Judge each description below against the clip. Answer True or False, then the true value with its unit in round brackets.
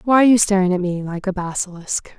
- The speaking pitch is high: True (195 Hz)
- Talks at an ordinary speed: False (245 wpm)